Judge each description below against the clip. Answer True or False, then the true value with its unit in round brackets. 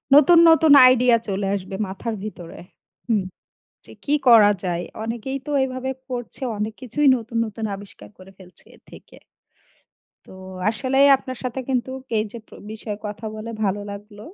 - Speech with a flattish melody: False (3.9 semitones)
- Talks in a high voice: True (225 Hz)